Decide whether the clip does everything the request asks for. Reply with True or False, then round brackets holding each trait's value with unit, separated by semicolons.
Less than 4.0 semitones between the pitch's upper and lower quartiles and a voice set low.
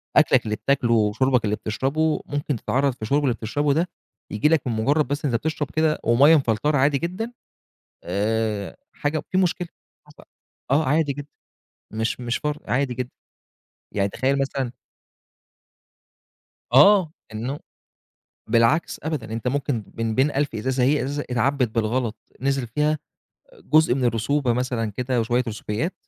False (4.3 semitones; 130 Hz)